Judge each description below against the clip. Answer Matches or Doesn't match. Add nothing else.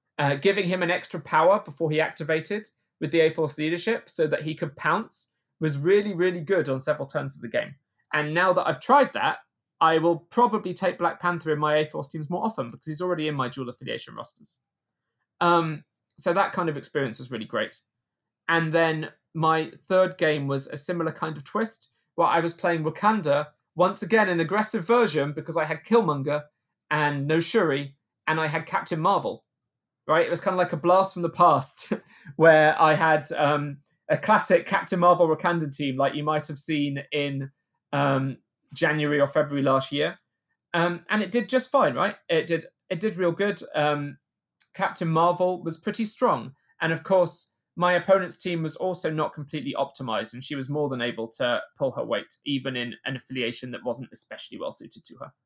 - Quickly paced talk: Doesn't match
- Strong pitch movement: Doesn't match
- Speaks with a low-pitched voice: Doesn't match